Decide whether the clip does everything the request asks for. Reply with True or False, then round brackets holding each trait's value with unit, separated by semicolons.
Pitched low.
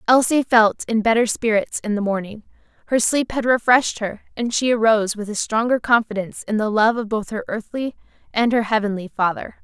False (225 Hz)